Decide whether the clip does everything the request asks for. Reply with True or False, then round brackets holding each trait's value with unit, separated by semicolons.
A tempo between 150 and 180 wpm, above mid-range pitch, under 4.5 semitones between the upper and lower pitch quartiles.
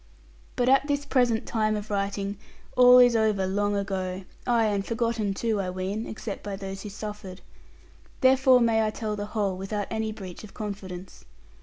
True (175 wpm; 210 Hz; 2.7 semitones)